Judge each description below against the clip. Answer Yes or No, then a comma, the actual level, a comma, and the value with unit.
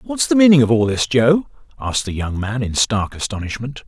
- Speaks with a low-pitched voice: Yes, low, 125 Hz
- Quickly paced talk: Yes, fast, 215 wpm